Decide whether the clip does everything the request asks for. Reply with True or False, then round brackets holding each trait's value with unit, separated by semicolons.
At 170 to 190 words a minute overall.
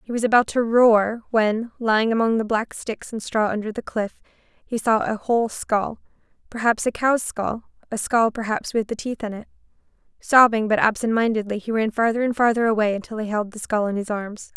False (205 wpm)